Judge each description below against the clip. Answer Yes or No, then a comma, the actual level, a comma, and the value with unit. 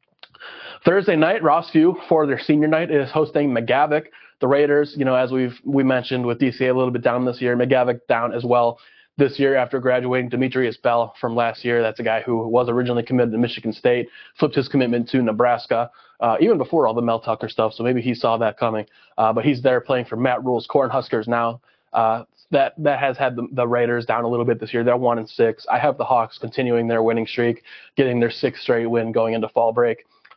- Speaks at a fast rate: Yes, fast, 225 wpm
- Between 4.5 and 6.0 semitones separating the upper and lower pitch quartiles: No, narrow, 2.4 semitones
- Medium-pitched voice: No, low, 125 Hz